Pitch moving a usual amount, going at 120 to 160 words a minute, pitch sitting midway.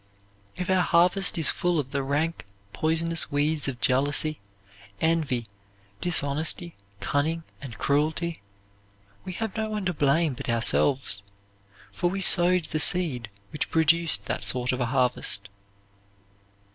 Yes: average, 4.1 semitones; slow, 135 wpm; medium, 155 Hz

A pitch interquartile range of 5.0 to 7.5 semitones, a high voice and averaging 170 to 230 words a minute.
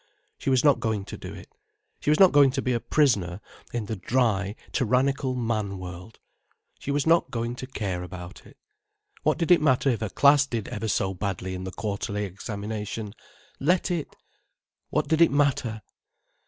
No: wide, 5.6 semitones; low, 115 Hz; average, 180 wpm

